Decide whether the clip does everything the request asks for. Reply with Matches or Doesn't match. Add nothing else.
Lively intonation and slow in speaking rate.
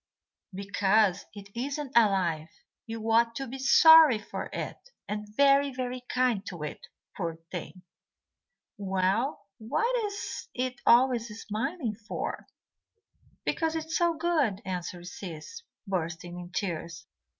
Matches